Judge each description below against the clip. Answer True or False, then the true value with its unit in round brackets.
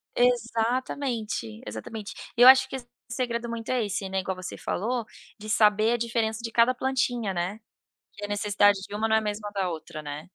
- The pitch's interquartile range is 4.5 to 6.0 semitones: False (3.0 semitones)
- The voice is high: True (220 Hz)